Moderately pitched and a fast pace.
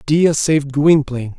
No: medium, 145 Hz; slow, 130 wpm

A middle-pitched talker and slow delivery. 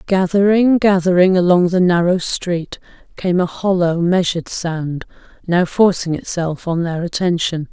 Yes: medium, 175 Hz; slow, 130 wpm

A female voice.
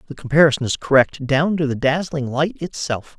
No: male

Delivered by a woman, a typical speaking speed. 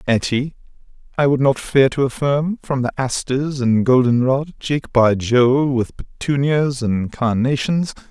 No: male; average, 150 wpm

